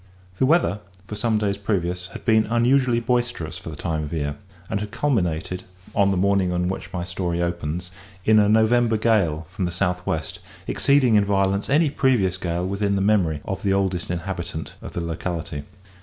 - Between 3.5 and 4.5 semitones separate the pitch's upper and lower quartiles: Yes, average, 3.9 semitones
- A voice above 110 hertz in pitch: No, very low, 95 Hz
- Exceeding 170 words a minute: Yes, average, 185 wpm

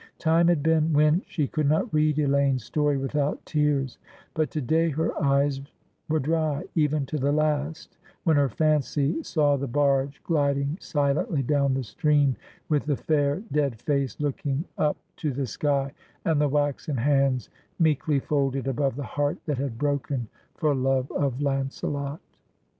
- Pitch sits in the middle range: Yes, medium, 145 Hz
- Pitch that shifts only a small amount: Yes, narrow, 1.8 semitones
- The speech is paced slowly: No, average, 160 wpm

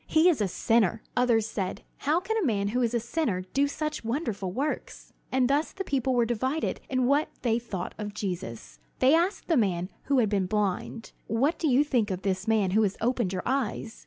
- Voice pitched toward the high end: Yes, high, 235 Hz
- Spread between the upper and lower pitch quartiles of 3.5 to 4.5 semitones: No, wide, 5.4 semitones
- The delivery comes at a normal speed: No, fast, 215 wpm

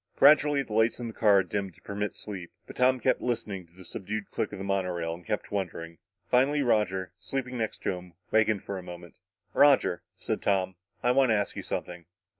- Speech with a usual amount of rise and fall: Yes, average, 4.7 semitones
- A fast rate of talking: Yes, fast, 210 wpm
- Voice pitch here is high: No, low, 105 Hz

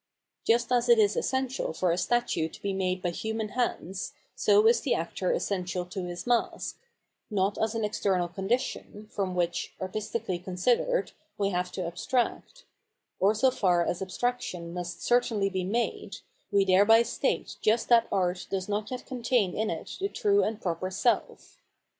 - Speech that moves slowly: No, average, 170 wpm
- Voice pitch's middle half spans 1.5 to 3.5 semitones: No, average, 4.6 semitones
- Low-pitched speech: No, high, 205 Hz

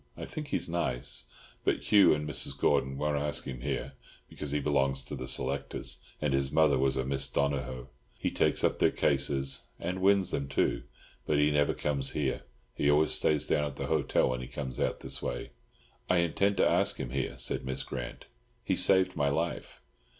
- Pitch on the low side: Yes, very low, 70 Hz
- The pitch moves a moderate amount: No, narrow, 2.1 semitones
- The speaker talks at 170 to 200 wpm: Yes, average, 195 wpm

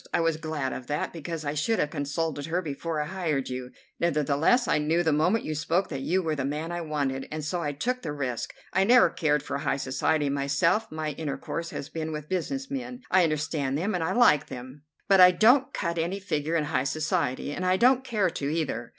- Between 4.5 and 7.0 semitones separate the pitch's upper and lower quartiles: No, average, 3.9 semitones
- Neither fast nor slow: No, fast, 225 wpm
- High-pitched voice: No, medium, 160 Hz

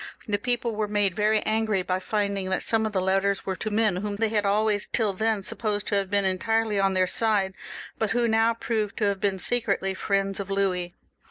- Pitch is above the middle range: Yes, high, 205 Hz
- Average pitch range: No, narrow, 2.1 semitones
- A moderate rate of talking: No, fast, 220 wpm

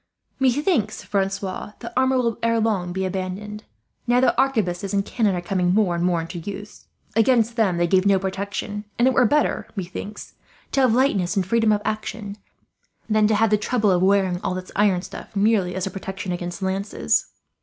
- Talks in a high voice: Yes, high, 200 Hz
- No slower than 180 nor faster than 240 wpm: Yes, average, 190 wpm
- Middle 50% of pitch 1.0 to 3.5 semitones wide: Yes, average, 3.2 semitones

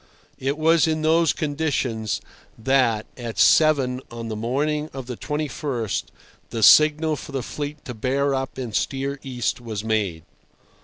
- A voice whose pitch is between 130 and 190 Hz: Yes, low, 135 Hz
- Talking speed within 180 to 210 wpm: No, average, 150 wpm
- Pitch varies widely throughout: No, average, 4.4 semitones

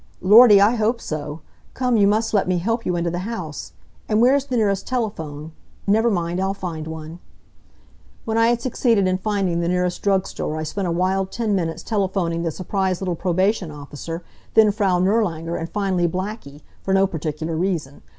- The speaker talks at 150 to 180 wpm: No, average, 190 wpm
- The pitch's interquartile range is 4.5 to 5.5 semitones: No, average, 4.0 semitones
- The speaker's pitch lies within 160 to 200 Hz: Yes, medium, 185 Hz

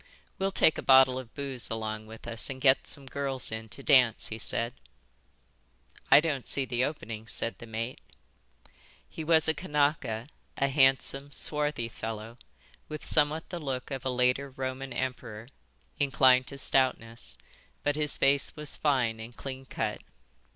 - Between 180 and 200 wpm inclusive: No, average, 160 wpm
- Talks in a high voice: No, low, 130 Hz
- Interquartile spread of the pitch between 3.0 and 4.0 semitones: Yes, average, 3.4 semitones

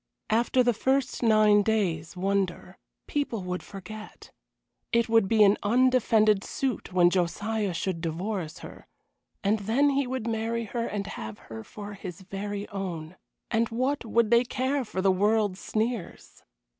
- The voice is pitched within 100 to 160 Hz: No, high, 215 Hz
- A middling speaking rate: Yes, average, 150 wpm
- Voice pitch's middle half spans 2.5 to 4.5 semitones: Yes, average, 3.5 semitones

